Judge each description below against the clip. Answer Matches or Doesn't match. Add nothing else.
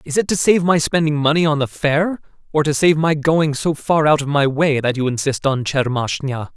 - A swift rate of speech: Matches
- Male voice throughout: Matches